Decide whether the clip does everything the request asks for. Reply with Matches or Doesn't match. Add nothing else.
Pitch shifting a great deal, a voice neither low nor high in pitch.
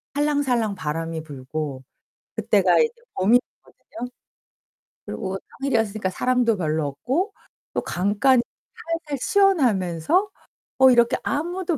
Doesn't match